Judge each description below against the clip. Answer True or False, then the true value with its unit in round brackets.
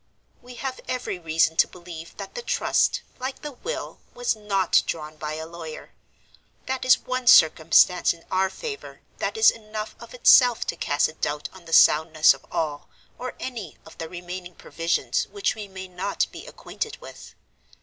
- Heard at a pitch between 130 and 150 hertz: False (185 Hz)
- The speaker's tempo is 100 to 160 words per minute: False (175 wpm)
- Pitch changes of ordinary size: False (7.5 semitones)